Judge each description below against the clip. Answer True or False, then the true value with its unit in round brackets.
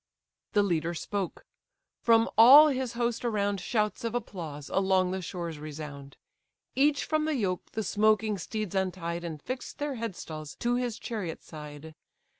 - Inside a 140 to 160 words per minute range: True (150 wpm)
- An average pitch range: False (5.8 semitones)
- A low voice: False (200 Hz)